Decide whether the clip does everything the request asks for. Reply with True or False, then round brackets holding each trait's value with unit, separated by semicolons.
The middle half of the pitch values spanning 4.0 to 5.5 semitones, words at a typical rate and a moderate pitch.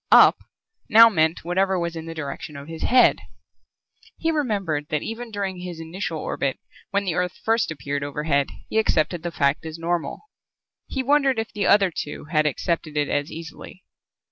True (4.9 semitones; 175 wpm; 170 Hz)